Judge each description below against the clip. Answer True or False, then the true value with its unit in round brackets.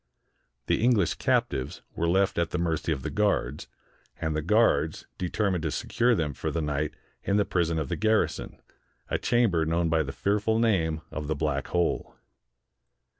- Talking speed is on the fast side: False (175 wpm)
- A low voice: True (85 Hz)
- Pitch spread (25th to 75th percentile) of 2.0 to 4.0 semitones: False (4.8 semitones)